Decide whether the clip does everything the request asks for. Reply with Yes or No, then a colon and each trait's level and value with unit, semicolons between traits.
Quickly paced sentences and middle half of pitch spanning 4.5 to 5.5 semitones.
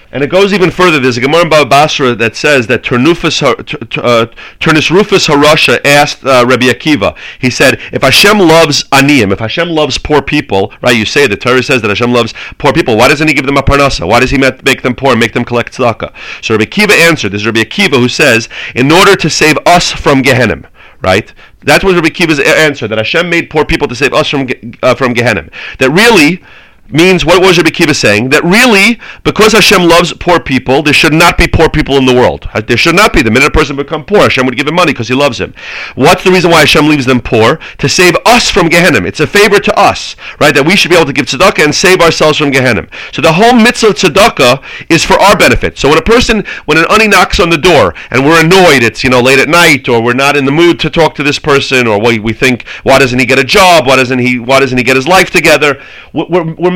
Yes: fast, 250 wpm; average, 5.0 semitones